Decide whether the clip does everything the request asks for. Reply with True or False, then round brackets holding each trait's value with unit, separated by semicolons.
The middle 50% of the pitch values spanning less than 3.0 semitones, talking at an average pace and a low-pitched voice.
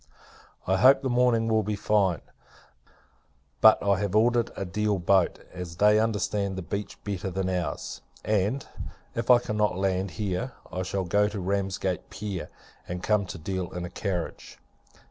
True (2.5 semitones; 165 wpm; 100 Hz)